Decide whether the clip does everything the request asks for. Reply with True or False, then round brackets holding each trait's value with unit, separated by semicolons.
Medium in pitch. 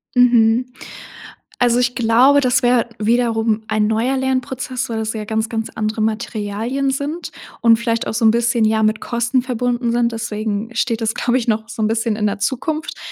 False (230 Hz)